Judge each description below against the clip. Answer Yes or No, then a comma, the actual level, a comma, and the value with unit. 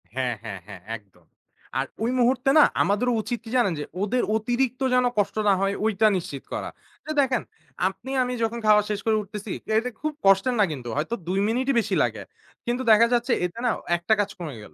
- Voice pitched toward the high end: Yes, high, 215 Hz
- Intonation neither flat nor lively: No, wide, 5.8 semitones